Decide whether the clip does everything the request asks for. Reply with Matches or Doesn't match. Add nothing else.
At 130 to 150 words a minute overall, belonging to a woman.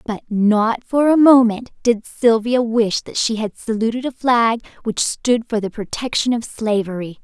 Doesn't match